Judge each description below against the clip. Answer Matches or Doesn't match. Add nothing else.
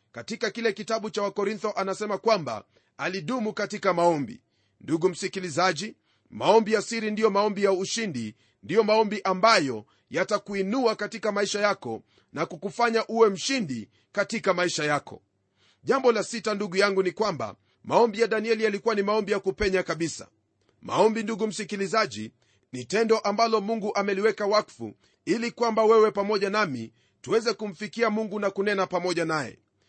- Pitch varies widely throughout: Doesn't match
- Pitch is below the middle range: Doesn't match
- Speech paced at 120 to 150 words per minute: Matches